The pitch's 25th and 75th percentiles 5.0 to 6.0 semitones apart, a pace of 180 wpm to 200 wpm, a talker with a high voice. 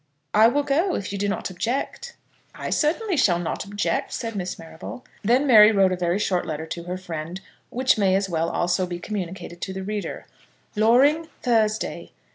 Yes: average, 5.3 semitones; average, 185 wpm; high, 200 Hz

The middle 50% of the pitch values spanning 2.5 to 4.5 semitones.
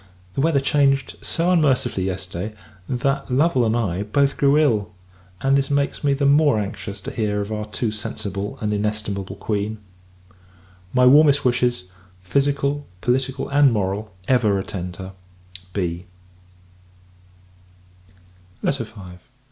No: wide, 5.4 semitones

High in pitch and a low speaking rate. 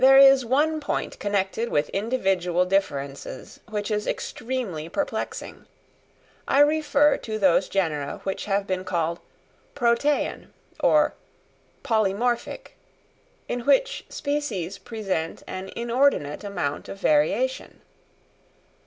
Yes: high, 210 Hz; slow, 105 wpm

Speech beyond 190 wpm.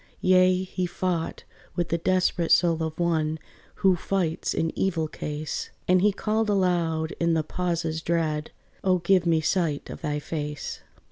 No: average, 155 wpm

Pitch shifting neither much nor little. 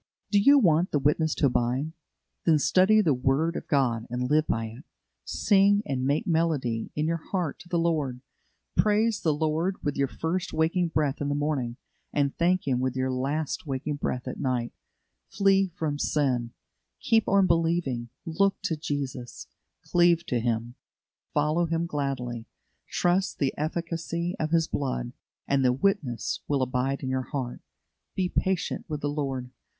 Yes: average, 4.6 semitones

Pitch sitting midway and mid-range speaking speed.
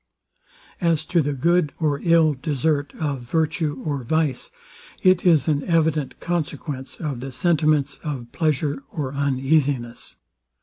No: medium, 150 Hz; slow, 130 wpm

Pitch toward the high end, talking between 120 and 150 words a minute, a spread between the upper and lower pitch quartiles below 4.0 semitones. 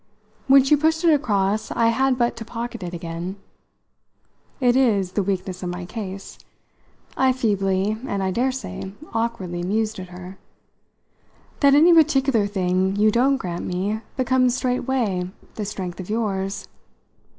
No: high, 215 Hz; average, 145 wpm; average, 5.3 semitones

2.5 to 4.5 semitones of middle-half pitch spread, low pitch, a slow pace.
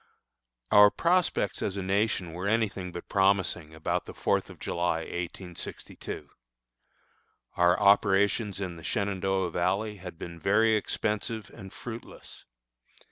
Yes: average, 2.8 semitones; very low, 95 Hz; slow, 130 wpm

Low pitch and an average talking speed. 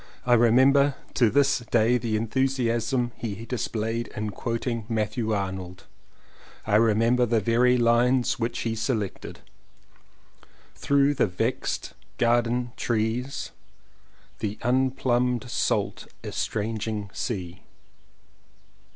No: low, 115 Hz; slow, 100 wpm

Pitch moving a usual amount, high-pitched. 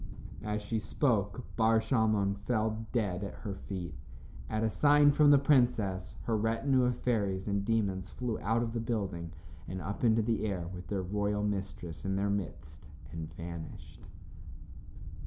No: average, 3.1 semitones; low, 105 Hz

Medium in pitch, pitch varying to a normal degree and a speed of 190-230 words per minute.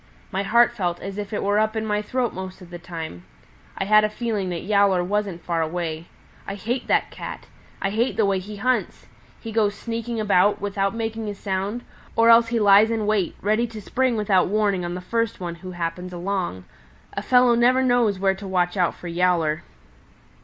No: high, 200 Hz; average, 3.6 semitones; fast, 205 wpm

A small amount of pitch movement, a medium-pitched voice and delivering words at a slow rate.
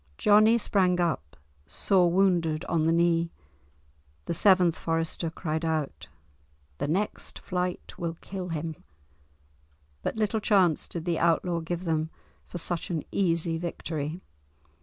Yes: narrow, 2.1 semitones; medium, 170 Hz; slow, 130 wpm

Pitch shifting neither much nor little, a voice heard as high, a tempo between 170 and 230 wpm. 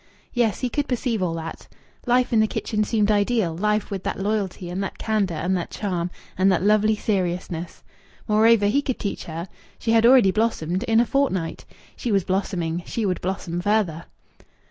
Yes: average, 3.7 semitones; high, 205 Hz; average, 185 wpm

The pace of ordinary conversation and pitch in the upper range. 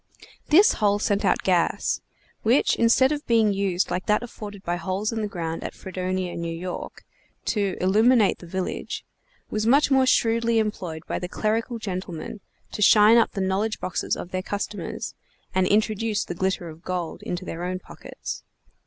Yes: average, 170 wpm; high, 200 Hz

